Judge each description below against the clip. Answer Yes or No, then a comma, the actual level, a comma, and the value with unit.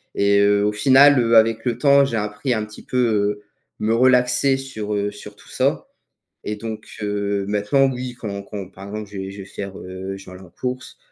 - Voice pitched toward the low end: Yes, low, 105 Hz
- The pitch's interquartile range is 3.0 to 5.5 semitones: Yes, average, 3.5 semitones